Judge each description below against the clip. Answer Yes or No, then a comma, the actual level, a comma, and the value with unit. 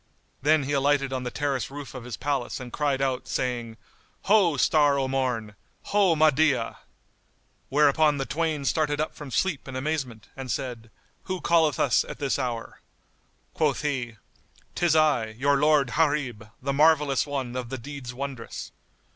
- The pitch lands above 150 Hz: No, medium, 140 Hz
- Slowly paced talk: No, average, 160 wpm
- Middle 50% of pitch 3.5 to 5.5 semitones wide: No, average, 2.9 semitones